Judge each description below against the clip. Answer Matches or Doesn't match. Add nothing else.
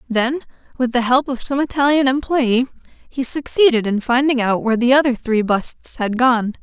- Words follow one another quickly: Doesn't match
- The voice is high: Matches